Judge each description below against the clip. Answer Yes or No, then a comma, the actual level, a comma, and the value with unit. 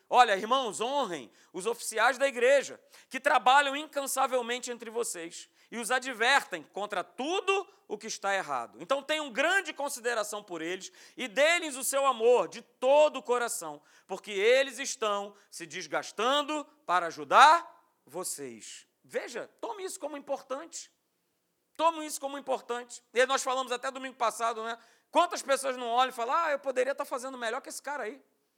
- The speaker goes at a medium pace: Yes, average, 160 wpm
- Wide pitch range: No, average, 4.4 semitones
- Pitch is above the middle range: Yes, very high, 260 Hz